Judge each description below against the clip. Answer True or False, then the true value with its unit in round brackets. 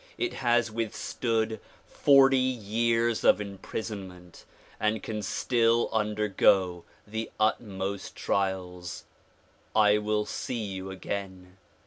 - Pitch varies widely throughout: False (3.0 semitones)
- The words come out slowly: True (95 wpm)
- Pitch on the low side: True (105 Hz)